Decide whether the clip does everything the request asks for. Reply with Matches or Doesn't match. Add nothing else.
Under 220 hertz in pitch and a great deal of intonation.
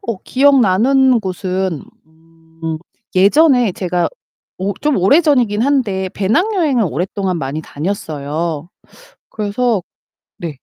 Matches